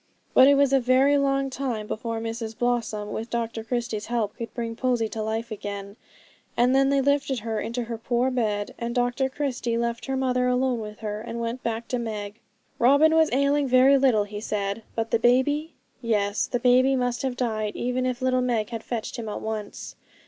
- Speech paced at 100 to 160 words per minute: No, average, 200 wpm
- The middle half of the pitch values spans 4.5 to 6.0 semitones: No, narrow, 2.6 semitones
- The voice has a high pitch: Yes, high, 240 Hz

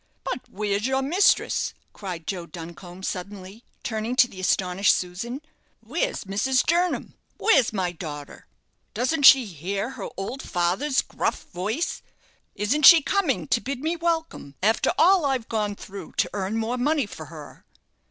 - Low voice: No, high, 215 Hz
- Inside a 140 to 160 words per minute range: Yes, average, 150 wpm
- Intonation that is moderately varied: No, wide, 6.4 semitones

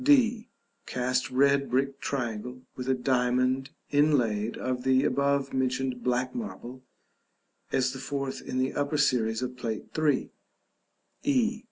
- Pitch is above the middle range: No, low, 130 Hz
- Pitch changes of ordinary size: No, narrow, 1.9 semitones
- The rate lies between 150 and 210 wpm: No, slow, 135 wpm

